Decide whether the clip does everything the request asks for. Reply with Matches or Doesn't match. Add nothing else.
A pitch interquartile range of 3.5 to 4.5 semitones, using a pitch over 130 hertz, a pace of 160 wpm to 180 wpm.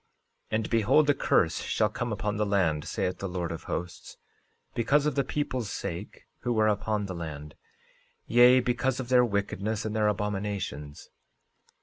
Doesn't match